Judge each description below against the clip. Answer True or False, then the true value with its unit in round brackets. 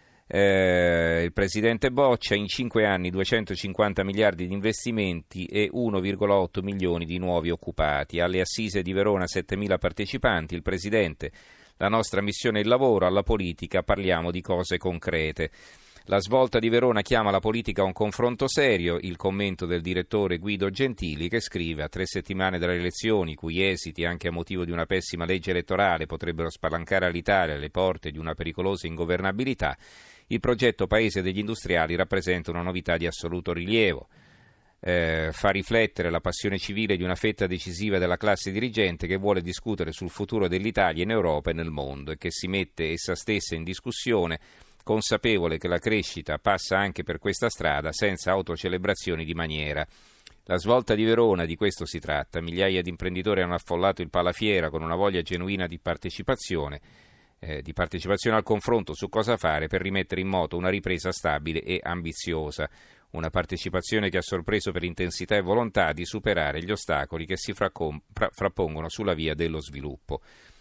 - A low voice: True (95 Hz)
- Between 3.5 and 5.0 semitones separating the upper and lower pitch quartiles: False (3.1 semitones)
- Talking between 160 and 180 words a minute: True (165 wpm)